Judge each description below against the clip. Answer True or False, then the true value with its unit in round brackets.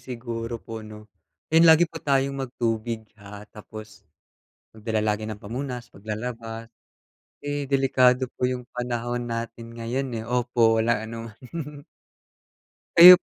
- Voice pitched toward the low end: True (120 Hz)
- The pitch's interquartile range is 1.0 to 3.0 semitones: True (2.6 semitones)